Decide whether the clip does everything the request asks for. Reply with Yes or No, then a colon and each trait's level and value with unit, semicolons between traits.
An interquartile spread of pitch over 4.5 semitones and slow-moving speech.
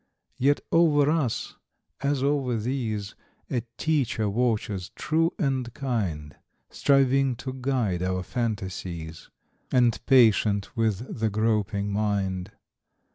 Yes: average, 5.1 semitones; slow, 105 wpm